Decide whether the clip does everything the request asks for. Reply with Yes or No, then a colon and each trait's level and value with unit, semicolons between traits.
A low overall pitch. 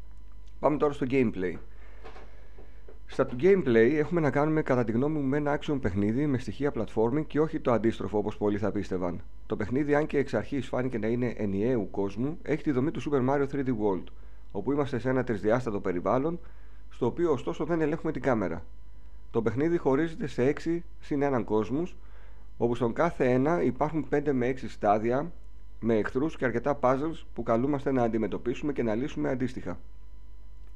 Yes: low, 120 Hz